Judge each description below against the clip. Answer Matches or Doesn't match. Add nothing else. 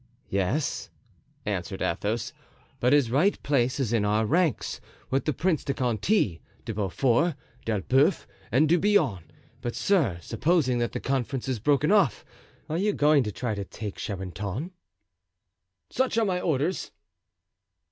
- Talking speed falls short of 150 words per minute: Matches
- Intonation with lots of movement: Matches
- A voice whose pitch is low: Matches